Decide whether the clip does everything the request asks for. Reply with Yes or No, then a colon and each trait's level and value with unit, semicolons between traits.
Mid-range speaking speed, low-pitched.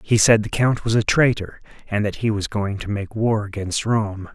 No: fast, 235 wpm; low, 105 Hz